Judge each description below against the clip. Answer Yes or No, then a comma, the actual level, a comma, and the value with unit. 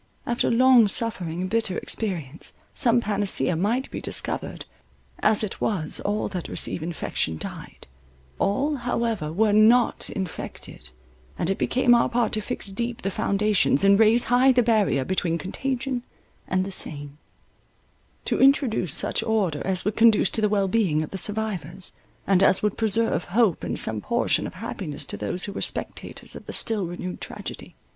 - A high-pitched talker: Yes, high, 205 Hz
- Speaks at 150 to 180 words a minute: Yes, average, 165 wpm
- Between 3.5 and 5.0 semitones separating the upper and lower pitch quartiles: Yes, average, 4.3 semitones